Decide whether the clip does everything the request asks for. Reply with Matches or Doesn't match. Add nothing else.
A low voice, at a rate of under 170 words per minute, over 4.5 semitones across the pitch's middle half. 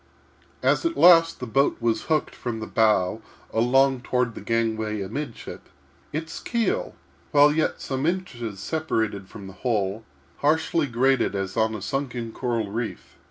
Matches